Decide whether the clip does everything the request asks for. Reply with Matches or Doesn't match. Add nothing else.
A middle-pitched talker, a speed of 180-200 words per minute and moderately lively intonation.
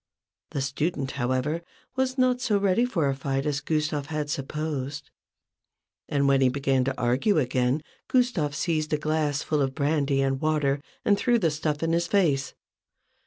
Doesn't match